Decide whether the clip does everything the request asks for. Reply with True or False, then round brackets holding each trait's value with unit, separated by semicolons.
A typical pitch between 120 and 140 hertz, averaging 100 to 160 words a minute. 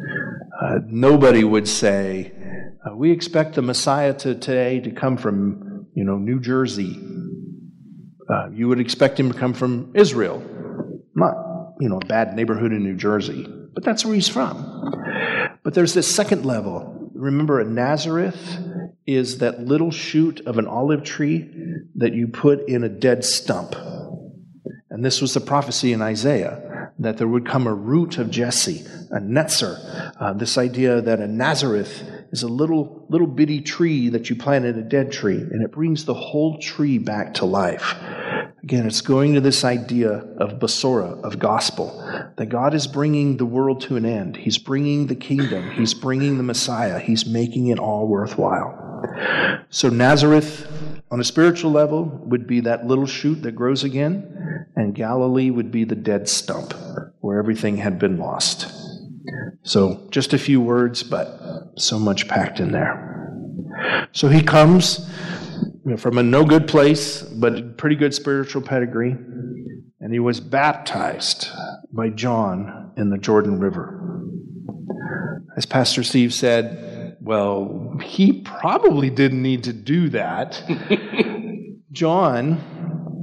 True (135 Hz; 155 wpm)